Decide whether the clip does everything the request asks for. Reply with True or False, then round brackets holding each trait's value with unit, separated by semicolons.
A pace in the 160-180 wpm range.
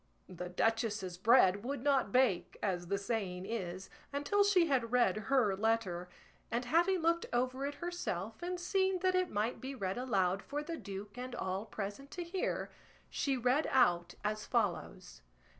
True (165 wpm)